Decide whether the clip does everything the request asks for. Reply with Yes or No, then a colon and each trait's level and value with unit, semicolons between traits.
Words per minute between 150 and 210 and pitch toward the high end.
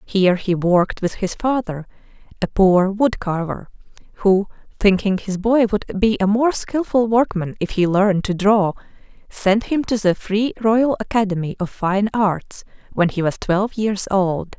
Yes: average, 170 wpm; high, 200 Hz